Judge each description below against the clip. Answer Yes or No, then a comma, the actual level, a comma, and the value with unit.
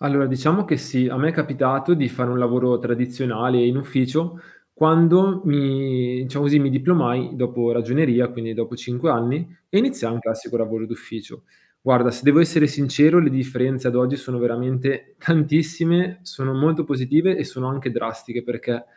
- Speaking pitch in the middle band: No, low, 130 Hz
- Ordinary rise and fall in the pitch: Yes, average, 3.7 semitones